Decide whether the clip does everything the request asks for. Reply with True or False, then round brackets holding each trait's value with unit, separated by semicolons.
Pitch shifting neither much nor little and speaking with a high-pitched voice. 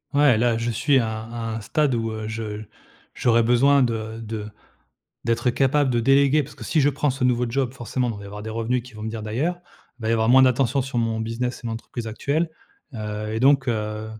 False (3.1 semitones; 115 Hz)